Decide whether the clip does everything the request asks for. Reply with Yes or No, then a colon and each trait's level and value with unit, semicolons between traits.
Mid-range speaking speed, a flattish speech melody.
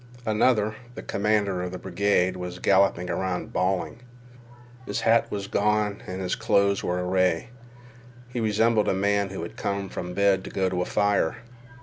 Yes: average, 170 wpm; narrow, 2.2 semitones